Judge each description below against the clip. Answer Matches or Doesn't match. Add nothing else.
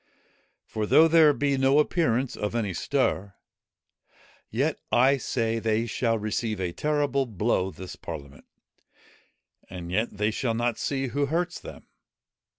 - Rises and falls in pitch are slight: Doesn't match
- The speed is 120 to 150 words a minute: Matches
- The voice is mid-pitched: Doesn't match